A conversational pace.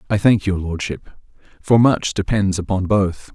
Yes: average, 160 wpm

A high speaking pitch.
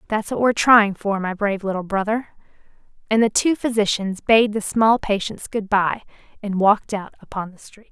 Yes: high, 210 Hz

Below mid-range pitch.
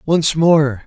No: medium, 150 Hz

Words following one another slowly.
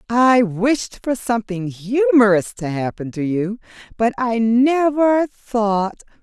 Yes: slow, 125 wpm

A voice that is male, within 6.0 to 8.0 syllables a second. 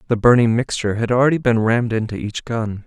Yes: male; 6.4 syllables/s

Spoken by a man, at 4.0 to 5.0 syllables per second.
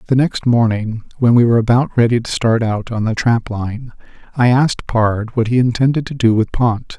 No: male; 5.2 syllables/s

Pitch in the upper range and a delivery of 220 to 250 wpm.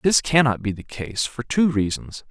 No: low, 120 Hz; fast, 235 wpm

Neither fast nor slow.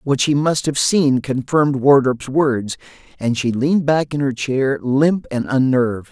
Yes: average, 175 wpm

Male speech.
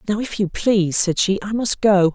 No: female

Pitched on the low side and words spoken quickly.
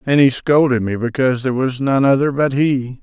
Yes: low, 130 Hz; fast, 220 wpm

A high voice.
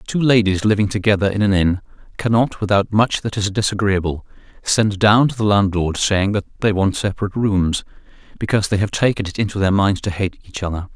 No: low, 100 Hz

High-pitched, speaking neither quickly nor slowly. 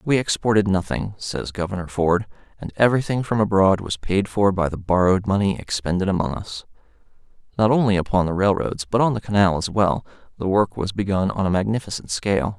No: low, 100 Hz; average, 185 wpm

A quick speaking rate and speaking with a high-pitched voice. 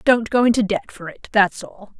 Yes: fast, 240 wpm; high, 205 Hz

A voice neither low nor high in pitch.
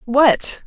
No: very high, 265 Hz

